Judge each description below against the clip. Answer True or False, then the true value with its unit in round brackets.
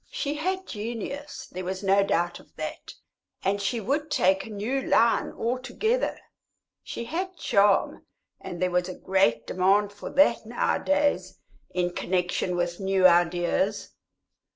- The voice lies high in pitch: True (200 Hz)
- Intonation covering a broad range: True (6.4 semitones)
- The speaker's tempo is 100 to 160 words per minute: True (140 wpm)